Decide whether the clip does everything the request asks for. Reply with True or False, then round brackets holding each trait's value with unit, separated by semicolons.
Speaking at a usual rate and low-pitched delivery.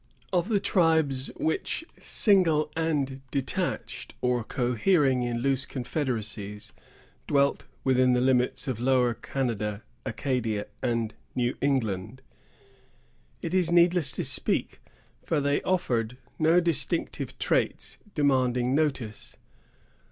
False (105 wpm; 130 Hz)